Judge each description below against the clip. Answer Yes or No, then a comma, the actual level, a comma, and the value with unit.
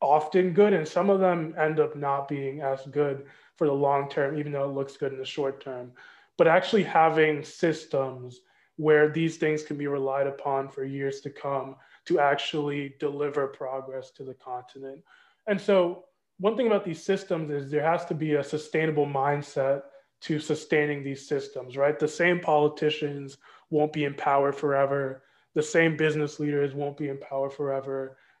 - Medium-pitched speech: Yes, medium, 145 Hz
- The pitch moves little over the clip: Yes, narrow, 2.2 semitones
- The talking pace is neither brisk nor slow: Yes, average, 175 wpm